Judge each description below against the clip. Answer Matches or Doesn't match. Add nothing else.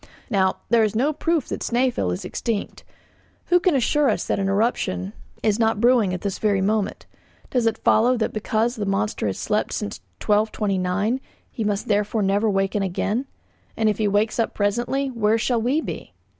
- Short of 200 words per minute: Matches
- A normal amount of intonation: Matches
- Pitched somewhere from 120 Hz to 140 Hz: Doesn't match